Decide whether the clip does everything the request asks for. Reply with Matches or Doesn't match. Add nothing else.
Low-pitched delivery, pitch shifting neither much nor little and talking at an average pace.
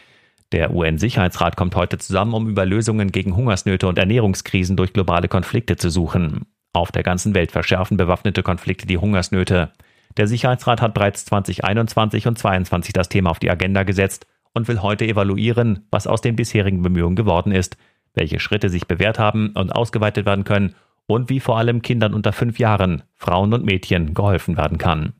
Matches